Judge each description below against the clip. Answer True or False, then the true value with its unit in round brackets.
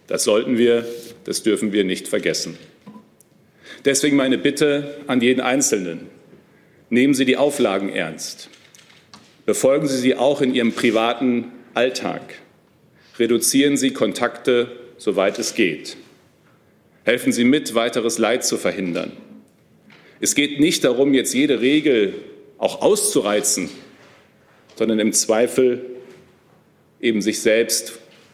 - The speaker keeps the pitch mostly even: False (3.7 semitones)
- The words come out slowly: True (115 wpm)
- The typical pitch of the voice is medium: False (130 Hz)